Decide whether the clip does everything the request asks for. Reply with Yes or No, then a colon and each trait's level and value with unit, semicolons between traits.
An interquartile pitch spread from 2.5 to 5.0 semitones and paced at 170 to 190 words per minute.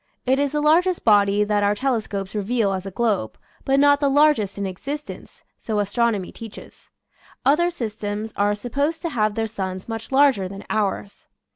No: wide, 5.4 semitones; average, 175 wpm